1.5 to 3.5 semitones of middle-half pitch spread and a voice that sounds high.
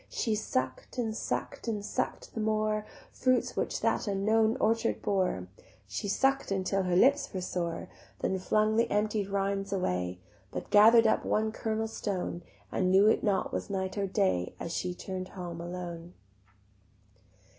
Yes: average, 3.1 semitones; high, 200 Hz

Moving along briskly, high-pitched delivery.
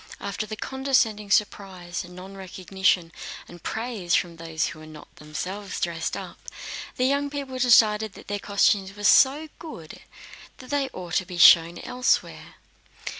No: average, 145 wpm; high, 195 Hz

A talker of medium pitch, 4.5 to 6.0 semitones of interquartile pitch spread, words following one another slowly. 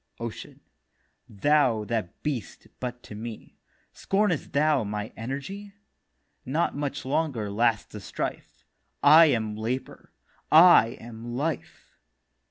No: low, 125 Hz; average, 5.3 semitones; slow, 110 wpm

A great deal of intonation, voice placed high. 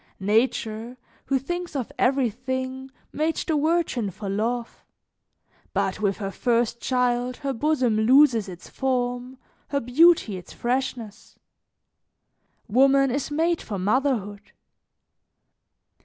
No: average, 3.7 semitones; very high, 250 Hz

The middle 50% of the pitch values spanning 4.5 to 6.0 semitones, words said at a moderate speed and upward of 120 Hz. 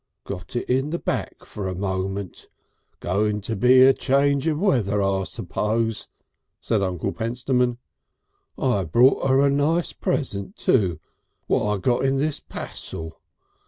No: wide, 5.5 semitones; average, 145 wpm; low, 115 Hz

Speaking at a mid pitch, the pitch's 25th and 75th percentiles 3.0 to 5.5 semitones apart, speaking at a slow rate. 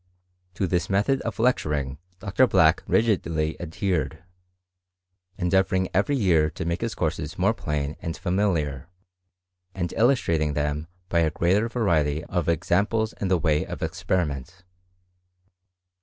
No: very low, 85 Hz; average, 4.3 semitones; slow, 125 wpm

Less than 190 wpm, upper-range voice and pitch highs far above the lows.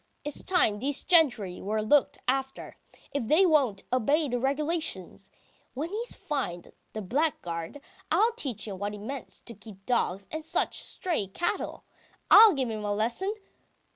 Yes: average, 155 wpm; very high, 265 Hz; wide, 6.9 semitones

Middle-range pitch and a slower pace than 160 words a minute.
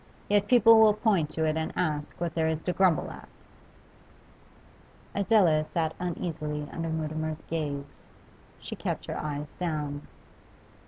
Yes: medium, 160 Hz; average, 140 wpm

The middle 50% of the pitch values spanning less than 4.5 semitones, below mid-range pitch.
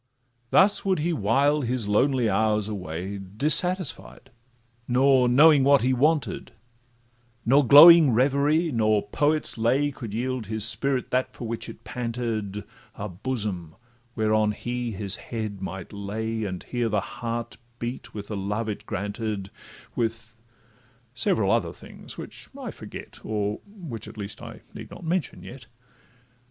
Yes: average, 4.1 semitones; low, 115 Hz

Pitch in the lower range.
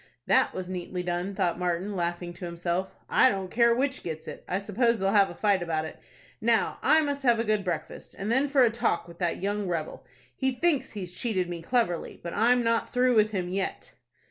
No: high, 195 Hz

